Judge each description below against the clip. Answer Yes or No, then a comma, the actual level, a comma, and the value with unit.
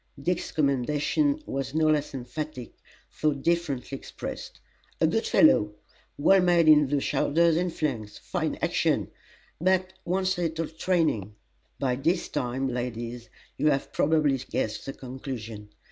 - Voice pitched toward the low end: No, medium, 145 Hz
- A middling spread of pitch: Yes, average, 4.8 semitones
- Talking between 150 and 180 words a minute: No, slow, 135 wpm